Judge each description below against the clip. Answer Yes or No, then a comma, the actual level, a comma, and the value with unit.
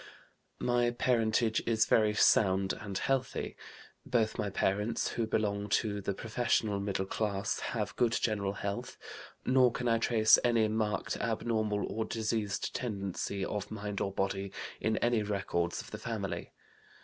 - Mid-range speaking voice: No, low, 110 Hz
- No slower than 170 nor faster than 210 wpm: No, average, 145 wpm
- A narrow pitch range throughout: Yes, narrow, 2.3 semitones